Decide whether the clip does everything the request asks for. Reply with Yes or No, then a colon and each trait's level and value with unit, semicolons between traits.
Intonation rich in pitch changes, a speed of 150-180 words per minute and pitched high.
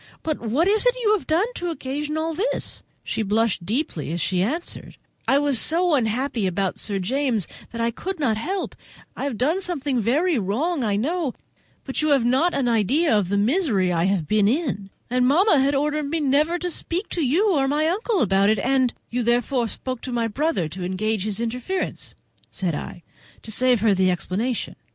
No: wide, 6.7 semitones; average, 195 wpm; very high, 255 Hz